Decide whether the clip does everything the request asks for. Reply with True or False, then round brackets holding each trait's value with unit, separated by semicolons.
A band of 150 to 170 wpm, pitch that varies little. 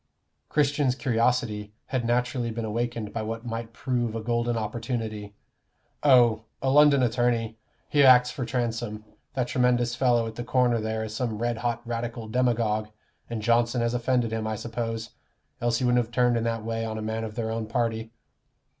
False (180 wpm; 1.6 semitones)